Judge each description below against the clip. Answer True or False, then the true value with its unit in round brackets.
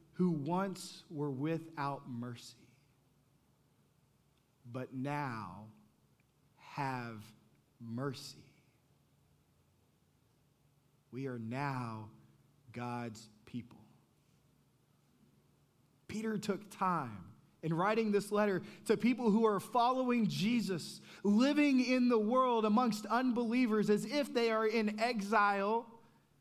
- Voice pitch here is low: False (170 Hz)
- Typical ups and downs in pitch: False (8.6 semitones)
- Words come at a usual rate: False (90 wpm)